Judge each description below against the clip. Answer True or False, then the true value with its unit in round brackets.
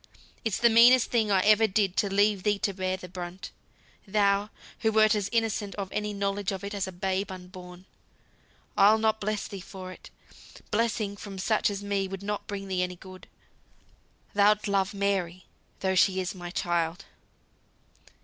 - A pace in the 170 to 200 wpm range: True (175 wpm)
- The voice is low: False (200 Hz)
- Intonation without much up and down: True (2.0 semitones)